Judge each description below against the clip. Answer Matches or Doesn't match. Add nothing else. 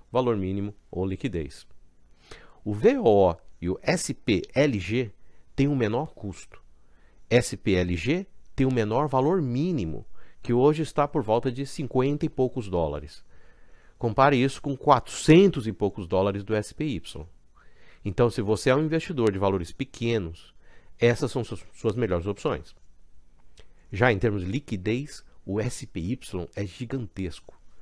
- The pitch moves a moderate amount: Doesn't match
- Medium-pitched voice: Doesn't match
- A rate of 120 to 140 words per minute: Matches